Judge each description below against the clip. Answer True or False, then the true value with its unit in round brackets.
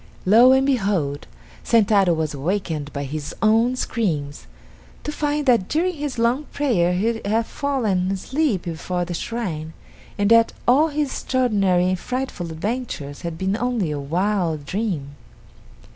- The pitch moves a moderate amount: False (6.6 semitones)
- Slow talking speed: False (145 wpm)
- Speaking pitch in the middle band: False (205 Hz)